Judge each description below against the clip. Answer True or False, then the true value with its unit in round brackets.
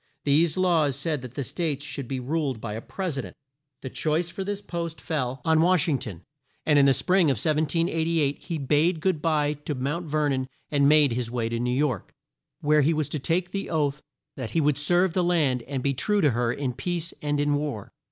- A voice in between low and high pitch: True (150 Hz)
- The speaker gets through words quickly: True (225 wpm)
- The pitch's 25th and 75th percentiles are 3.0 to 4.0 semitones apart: True (3.5 semitones)